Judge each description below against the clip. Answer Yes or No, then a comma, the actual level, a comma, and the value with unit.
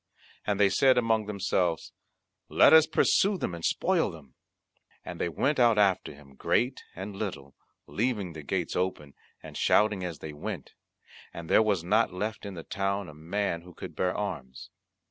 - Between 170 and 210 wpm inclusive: Yes, average, 175 wpm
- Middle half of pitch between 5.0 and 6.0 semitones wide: No, average, 4.4 semitones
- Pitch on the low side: Yes, very low, 95 Hz